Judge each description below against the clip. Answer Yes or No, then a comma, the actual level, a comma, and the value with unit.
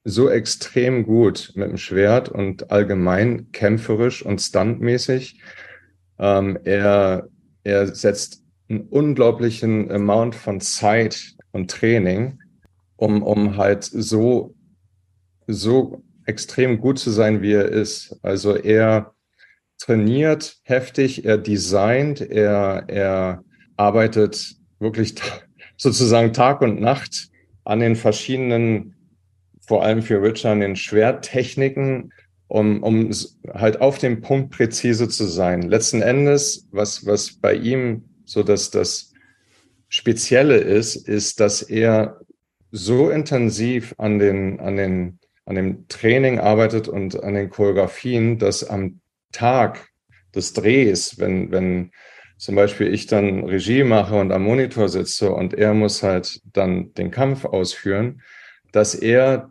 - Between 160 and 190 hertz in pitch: No, low, 110 Hz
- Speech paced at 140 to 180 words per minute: No, slow, 125 wpm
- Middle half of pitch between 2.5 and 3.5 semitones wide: Yes, average, 3.0 semitones